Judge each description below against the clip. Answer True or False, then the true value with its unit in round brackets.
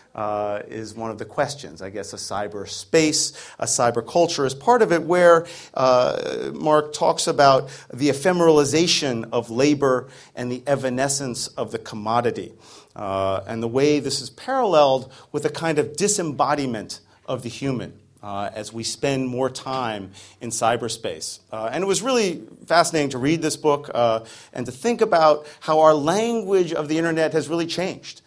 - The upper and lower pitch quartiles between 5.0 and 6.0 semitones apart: True (5.5 semitones)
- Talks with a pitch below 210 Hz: True (140 Hz)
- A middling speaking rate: True (165 wpm)